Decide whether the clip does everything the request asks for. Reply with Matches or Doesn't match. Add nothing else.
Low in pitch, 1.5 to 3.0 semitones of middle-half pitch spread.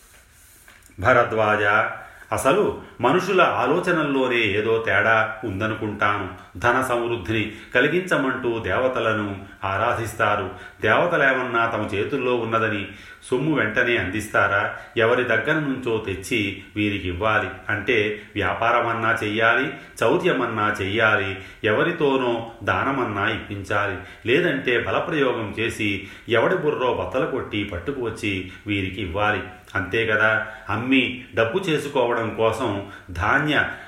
Matches